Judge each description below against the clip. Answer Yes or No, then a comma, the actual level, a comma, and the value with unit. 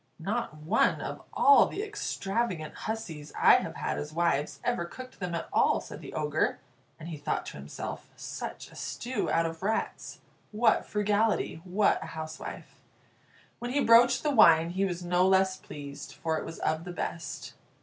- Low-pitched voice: No, medium, 175 Hz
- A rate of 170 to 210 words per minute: Yes, average, 175 wpm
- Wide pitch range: Yes, wide, 5.7 semitones